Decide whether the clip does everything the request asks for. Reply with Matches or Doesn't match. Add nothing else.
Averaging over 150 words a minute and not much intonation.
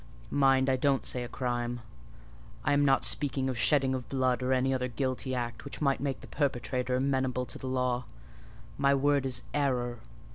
Matches